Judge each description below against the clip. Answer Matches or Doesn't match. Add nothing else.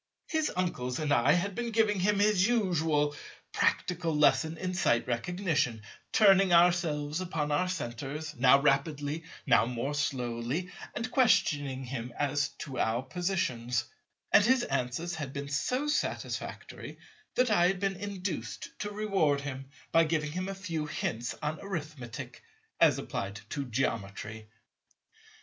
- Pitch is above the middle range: Doesn't match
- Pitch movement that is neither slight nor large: Doesn't match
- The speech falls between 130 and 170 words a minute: Matches